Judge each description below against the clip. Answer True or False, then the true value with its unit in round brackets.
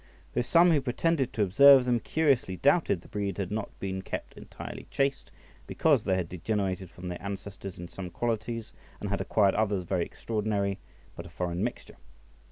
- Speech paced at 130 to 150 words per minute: False (175 wpm)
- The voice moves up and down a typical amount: True (4.8 semitones)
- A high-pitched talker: False (100 Hz)